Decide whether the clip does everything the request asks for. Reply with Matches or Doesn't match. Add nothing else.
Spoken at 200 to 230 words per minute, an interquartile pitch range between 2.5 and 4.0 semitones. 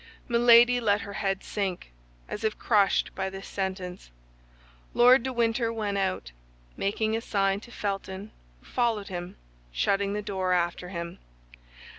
Doesn't match